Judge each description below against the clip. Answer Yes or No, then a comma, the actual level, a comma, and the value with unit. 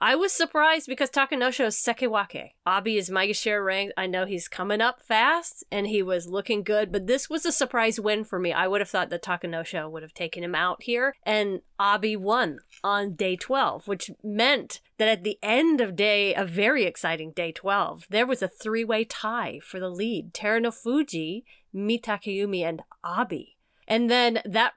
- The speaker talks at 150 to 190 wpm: Yes, average, 185 wpm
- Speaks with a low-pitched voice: No, high, 210 Hz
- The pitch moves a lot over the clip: No, average, 3.8 semitones